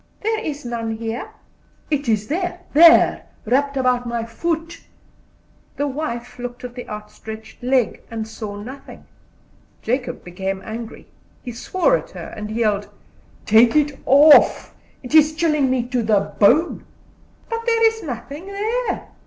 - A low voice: No, very high, 255 Hz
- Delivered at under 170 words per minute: Yes, average, 140 wpm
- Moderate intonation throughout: No, wide, 5.8 semitones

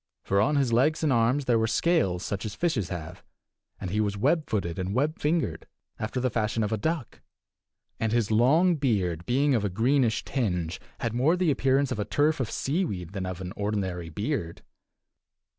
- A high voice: No, low, 115 Hz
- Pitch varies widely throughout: Yes, wide, 6.2 semitones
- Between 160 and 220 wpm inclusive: Yes, average, 190 wpm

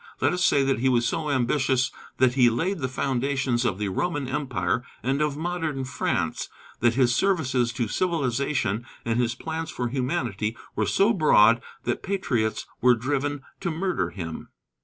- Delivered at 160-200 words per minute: Yes, average, 165 wpm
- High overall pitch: No, low, 130 Hz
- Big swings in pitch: No, average, 4.1 semitones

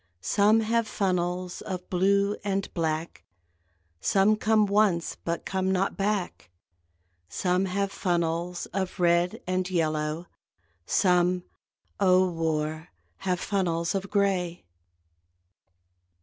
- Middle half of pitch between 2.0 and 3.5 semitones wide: Yes, narrow, 2.5 semitones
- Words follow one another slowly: Yes, slow, 105 wpm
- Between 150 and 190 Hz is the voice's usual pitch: Yes, medium, 185 Hz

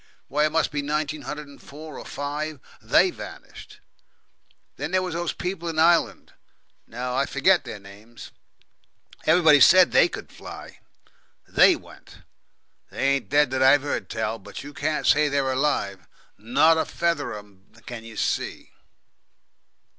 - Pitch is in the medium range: Yes, medium, 145 Hz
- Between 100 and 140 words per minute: No, average, 155 wpm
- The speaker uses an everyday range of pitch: Yes, average, 3.9 semitones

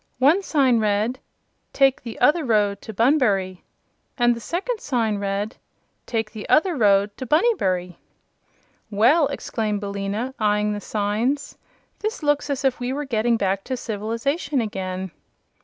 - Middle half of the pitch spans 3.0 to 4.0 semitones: No, average, 5.2 semitones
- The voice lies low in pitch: No, high, 230 Hz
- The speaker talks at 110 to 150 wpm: Yes, average, 140 wpm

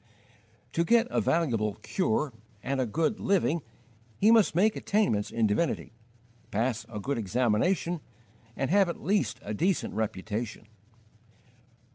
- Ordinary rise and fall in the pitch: No, wide, 8.9 semitones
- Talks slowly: Yes, slow, 130 wpm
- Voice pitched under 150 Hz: Yes, medium, 140 Hz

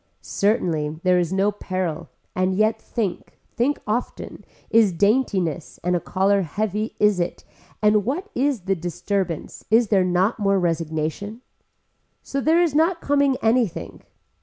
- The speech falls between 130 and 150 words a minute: Yes, average, 140 wpm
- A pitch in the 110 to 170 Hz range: No, high, 200 Hz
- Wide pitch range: No, average, 4.4 semitones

